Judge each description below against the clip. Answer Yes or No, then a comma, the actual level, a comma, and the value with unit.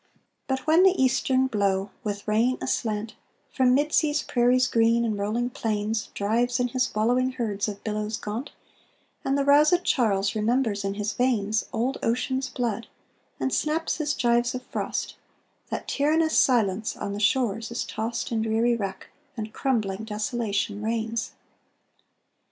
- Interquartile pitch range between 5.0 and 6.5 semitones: No, average, 3.4 semitones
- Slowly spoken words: No, average, 150 wpm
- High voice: Yes, high, 230 Hz